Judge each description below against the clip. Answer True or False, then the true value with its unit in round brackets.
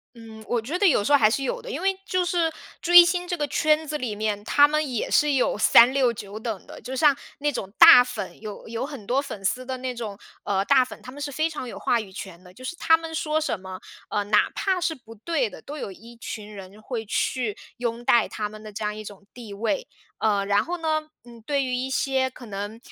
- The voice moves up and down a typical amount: False (5.8 semitones)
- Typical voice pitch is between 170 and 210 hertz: False (245 Hz)